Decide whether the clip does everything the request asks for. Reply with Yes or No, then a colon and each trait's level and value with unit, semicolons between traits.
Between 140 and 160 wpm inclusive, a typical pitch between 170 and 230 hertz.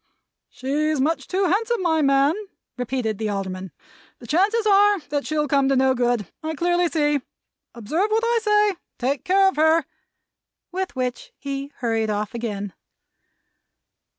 No: average, 150 wpm; very high, 290 Hz